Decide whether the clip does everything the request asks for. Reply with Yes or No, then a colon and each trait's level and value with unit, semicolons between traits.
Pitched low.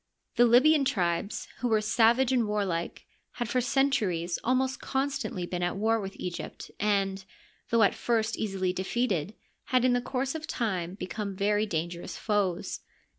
No: high, 210 Hz